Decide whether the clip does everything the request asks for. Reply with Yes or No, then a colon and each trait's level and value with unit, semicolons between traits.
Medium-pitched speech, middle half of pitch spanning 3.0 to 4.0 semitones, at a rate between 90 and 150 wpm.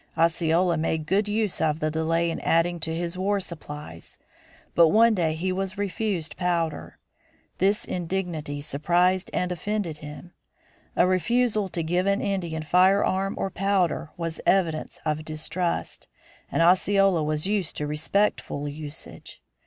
Yes: medium, 175 Hz; average, 3.3 semitones; average, 140 wpm